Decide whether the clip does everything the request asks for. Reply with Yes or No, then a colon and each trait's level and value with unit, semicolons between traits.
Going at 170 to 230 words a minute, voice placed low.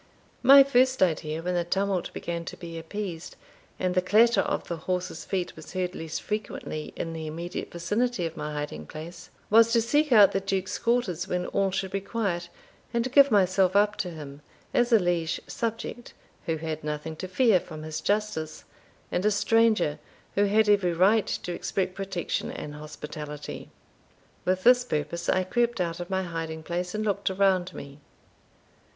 No: average, 175 wpm; medium, 185 Hz